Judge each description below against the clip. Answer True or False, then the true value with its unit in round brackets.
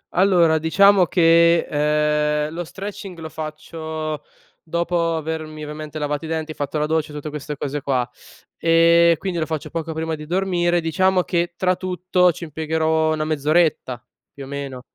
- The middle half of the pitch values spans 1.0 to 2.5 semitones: True (2.0 semitones)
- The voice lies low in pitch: False (160 Hz)